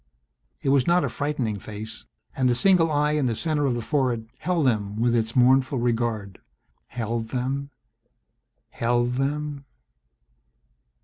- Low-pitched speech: Yes, low, 125 Hz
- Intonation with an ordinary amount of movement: Yes, average, 3.8 semitones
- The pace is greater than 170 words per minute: No, average, 140 wpm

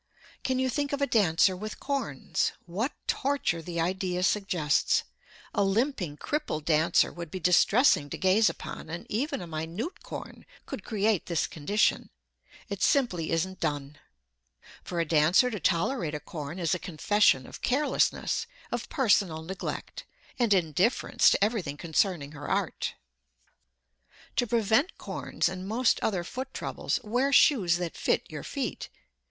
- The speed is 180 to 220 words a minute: No, average, 145 wpm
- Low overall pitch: No, medium, 185 Hz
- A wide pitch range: Yes, wide, 6.1 semitones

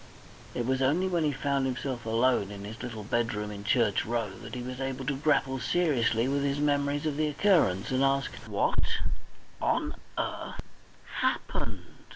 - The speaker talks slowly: No, average, 170 wpm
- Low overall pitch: Yes, low, 130 Hz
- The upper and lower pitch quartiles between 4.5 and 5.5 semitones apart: No, average, 3.7 semitones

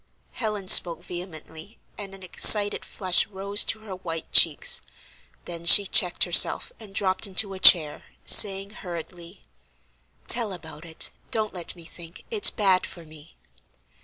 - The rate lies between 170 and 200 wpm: No, average, 145 wpm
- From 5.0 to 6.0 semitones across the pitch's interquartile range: No, average, 3.2 semitones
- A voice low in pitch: No, medium, 185 Hz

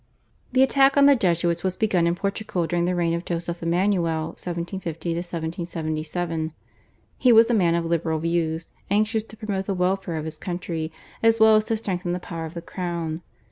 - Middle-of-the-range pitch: Yes, medium, 175 Hz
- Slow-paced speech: No, average, 185 wpm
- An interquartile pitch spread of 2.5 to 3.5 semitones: Yes, average, 3.0 semitones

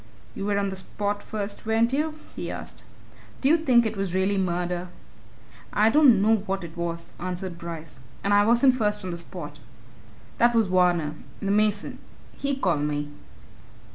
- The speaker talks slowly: No, average, 170 wpm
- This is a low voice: No, high, 200 Hz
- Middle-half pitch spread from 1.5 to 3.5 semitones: No, average, 4.1 semitones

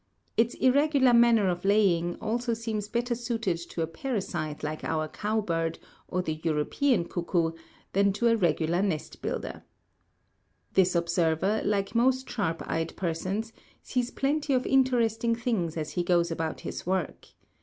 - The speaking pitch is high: Yes, high, 200 Hz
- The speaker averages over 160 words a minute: No, average, 150 wpm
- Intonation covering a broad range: Yes, wide, 5.8 semitones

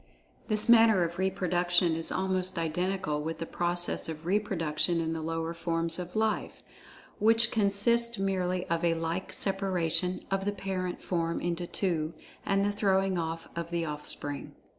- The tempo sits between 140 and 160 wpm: Yes, average, 155 wpm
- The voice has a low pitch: No, medium, 180 Hz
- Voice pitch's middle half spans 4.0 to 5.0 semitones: No, average, 2.8 semitones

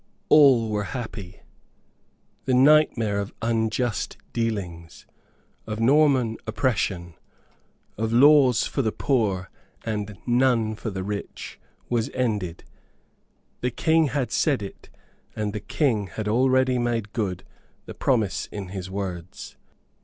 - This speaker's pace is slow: Yes, slow, 120 wpm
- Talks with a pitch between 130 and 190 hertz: No, low, 110 Hz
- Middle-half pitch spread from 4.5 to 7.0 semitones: No, average, 4.0 semitones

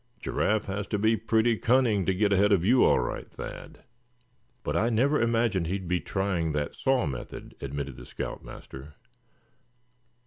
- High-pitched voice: No, low, 100 Hz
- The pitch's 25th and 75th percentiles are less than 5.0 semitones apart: No, average, 5.3 semitones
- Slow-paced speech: No, average, 165 wpm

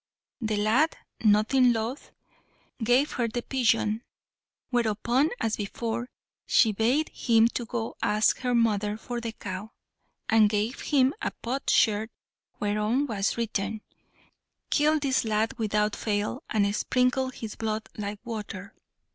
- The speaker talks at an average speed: No, slow, 125 wpm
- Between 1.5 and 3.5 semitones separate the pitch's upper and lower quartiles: Yes, average, 2.7 semitones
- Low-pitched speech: No, high, 225 Hz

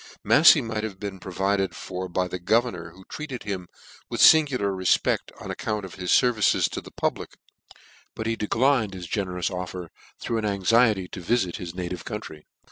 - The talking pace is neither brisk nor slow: Yes, average, 180 wpm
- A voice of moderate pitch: No, low, 100 Hz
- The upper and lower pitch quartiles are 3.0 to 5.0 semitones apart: Yes, average, 3.8 semitones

